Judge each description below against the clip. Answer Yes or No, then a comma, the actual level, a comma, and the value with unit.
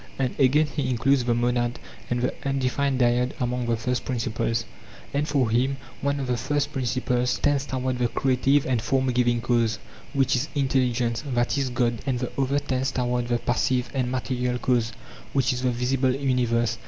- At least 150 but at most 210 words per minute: Yes, average, 180 wpm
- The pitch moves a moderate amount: No, narrow, 1.8 semitones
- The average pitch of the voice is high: No, low, 125 Hz